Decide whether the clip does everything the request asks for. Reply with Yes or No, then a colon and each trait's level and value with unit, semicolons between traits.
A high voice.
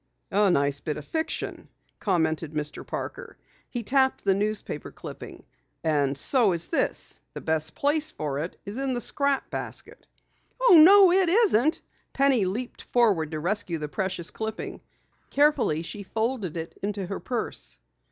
Yes: high, 205 Hz